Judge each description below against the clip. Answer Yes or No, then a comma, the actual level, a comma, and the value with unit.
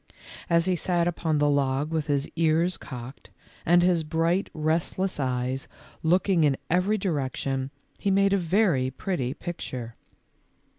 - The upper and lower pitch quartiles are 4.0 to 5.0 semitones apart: Yes, average, 4.7 semitones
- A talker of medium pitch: Yes, medium, 160 Hz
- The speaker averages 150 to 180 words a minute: No, average, 140 wpm